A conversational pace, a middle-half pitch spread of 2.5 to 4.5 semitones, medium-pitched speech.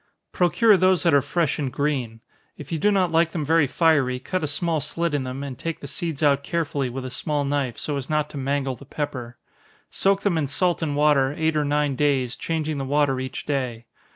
No: fast, 230 wpm; average, 3.2 semitones; medium, 145 Hz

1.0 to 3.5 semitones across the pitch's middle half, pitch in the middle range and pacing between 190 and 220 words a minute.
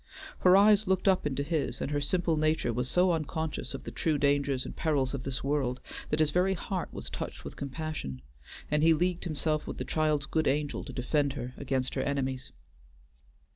Yes: average, 3.1 semitones; medium, 150 Hz; average, 200 wpm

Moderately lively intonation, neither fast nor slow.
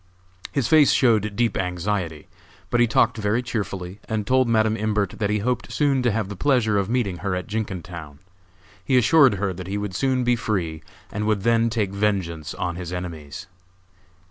Yes: average, 4.2 semitones; average, 185 wpm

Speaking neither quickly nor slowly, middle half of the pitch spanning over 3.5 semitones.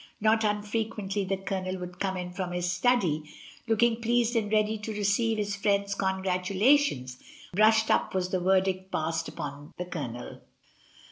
No: average, 160 wpm; average, 3.2 semitones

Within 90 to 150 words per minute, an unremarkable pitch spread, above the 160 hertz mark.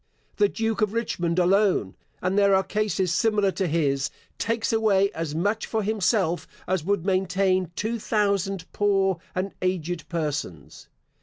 Yes: average, 145 wpm; average, 3.1 semitones; high, 190 Hz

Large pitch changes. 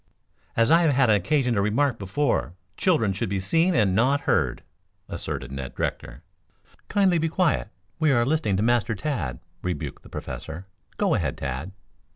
Yes: wide, 7.7 semitones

